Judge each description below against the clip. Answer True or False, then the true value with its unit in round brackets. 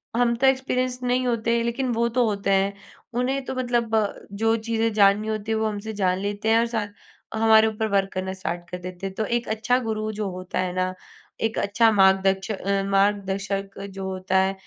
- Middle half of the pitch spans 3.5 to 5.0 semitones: False (2.9 semitones)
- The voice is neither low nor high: False (215 Hz)